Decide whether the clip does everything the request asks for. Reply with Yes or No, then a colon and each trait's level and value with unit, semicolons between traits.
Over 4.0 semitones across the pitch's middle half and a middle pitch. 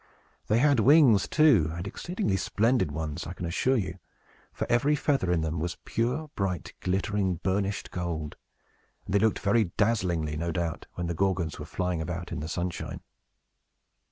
No: average, 5.0 semitones; very low, 95 Hz